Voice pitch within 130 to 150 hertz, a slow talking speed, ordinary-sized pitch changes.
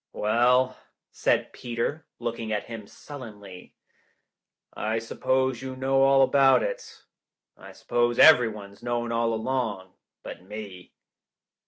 No: low, 120 Hz; slow, 115 wpm; average, 3.3 semitones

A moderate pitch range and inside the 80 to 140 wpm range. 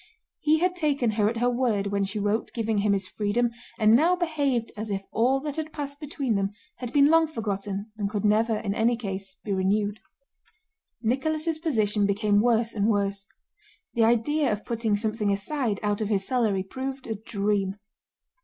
No: average, 4.4 semitones; average, 180 wpm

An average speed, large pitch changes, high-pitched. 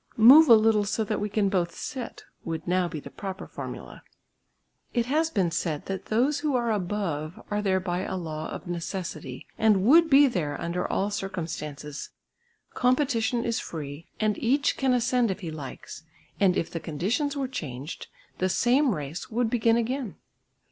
Yes: average, 175 wpm; wide, 6.1 semitones; high, 205 Hz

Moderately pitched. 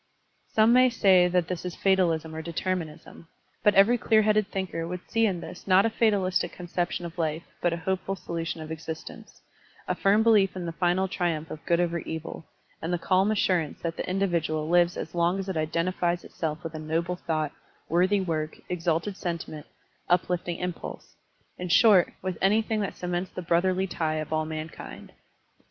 Yes: medium, 175 Hz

